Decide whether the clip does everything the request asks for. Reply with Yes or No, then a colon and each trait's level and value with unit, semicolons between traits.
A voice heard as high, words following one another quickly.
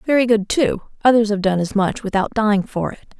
Yes: high, 210 Hz; fast, 225 wpm